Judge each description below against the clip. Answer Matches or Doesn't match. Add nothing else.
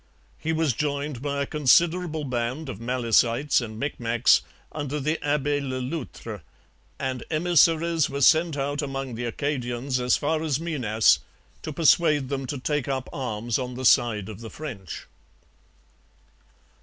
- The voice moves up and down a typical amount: Matches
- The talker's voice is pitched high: Doesn't match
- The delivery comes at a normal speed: Matches